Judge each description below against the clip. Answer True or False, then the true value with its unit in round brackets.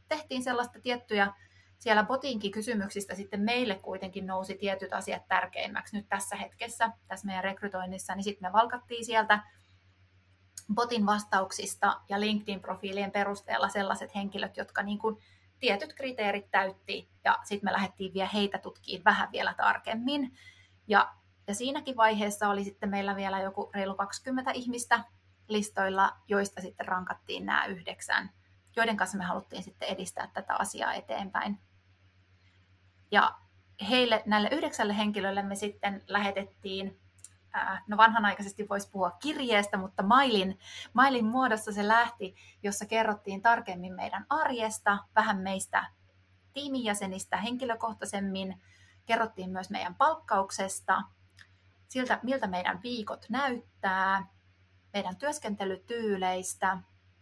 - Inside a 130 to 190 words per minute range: False (120 wpm)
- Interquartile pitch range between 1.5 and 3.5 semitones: True (3.1 semitones)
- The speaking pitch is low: False (200 Hz)